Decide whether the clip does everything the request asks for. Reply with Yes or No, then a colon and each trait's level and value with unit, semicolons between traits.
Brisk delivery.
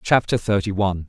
No: average, 165 wpm